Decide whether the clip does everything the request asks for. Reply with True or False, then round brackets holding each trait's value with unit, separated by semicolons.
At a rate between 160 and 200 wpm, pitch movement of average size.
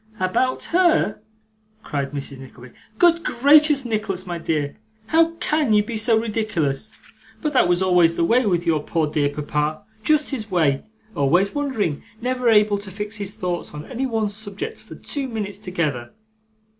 False (165 wpm; 7.3 semitones)